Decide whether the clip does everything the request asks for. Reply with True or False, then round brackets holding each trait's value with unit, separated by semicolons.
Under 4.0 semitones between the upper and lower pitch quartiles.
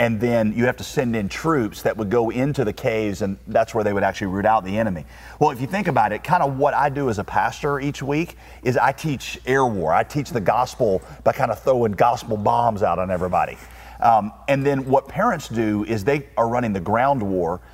False (5.3 semitones)